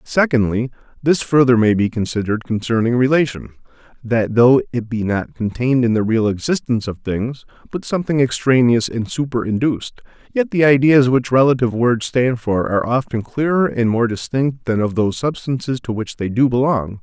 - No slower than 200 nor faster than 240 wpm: No, average, 170 wpm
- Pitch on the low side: Yes, low, 120 Hz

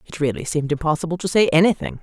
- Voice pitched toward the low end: No, medium, 160 Hz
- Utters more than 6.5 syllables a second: Yes, 7.3 syllables/s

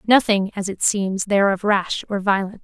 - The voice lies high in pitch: Yes, high, 200 Hz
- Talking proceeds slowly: No, fast, 205 wpm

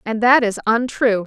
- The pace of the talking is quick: No, average, 190 wpm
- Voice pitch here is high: Yes, high, 225 Hz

